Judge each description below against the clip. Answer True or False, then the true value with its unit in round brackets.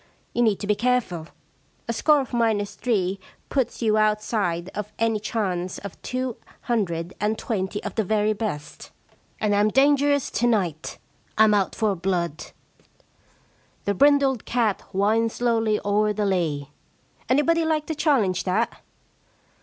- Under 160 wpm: True (145 wpm)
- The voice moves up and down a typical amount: True (3.7 semitones)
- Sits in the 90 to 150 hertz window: False (215 Hz)